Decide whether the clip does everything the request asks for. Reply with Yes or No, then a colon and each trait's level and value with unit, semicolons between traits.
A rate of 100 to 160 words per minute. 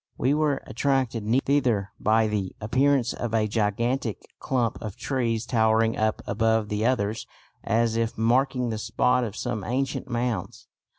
Yes: average, 145 wpm